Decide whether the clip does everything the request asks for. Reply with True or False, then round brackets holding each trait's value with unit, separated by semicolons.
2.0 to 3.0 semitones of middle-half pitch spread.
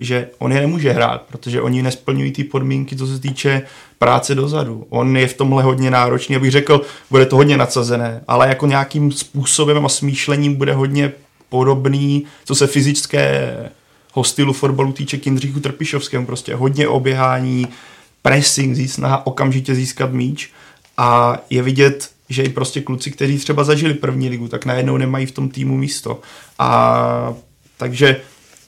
False (1.6 semitones)